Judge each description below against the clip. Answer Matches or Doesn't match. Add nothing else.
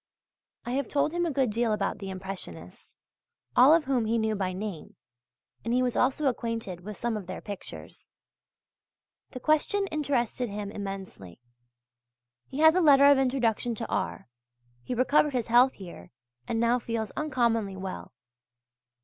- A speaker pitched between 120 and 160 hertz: Doesn't match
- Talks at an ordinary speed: Matches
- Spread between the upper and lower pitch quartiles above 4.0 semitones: Matches